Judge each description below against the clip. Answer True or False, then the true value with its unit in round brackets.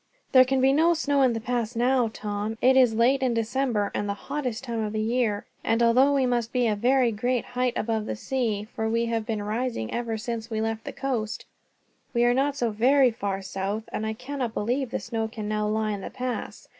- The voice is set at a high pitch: True (235 Hz)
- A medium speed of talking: False (230 wpm)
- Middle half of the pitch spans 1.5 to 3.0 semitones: True (2.7 semitones)